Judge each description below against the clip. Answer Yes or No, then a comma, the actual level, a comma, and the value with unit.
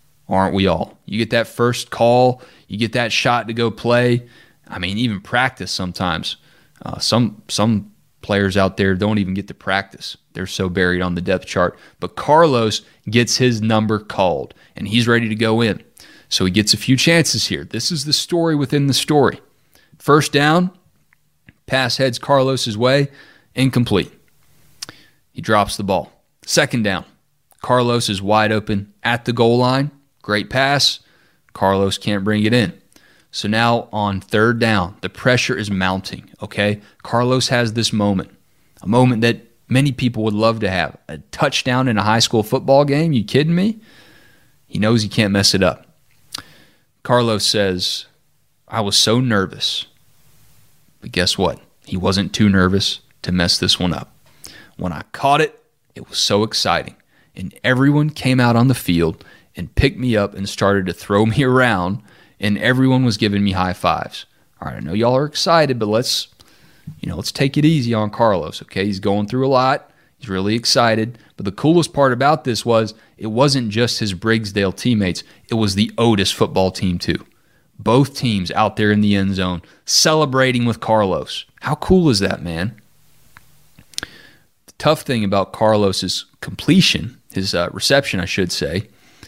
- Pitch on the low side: Yes, low, 115 Hz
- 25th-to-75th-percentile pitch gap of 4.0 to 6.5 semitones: Yes, average, 4.3 semitones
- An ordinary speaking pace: Yes, average, 175 wpm